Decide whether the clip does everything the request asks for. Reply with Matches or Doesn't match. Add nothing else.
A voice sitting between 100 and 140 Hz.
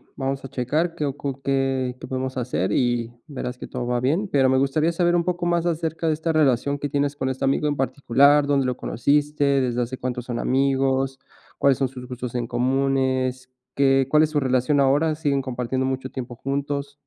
Matches